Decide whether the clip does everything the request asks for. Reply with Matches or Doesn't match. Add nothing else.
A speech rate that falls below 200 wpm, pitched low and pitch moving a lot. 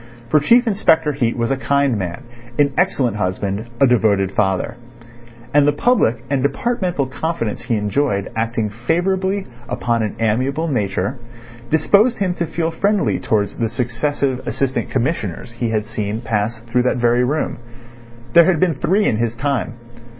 Matches